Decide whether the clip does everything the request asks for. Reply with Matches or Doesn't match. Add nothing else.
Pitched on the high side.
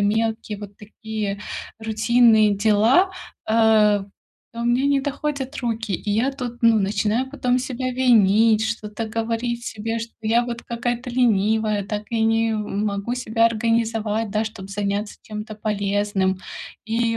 Matches